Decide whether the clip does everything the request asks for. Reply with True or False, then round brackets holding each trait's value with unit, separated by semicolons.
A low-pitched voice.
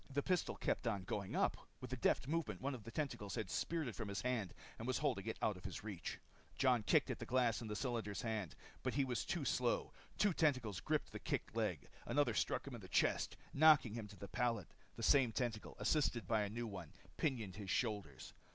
True (115 Hz)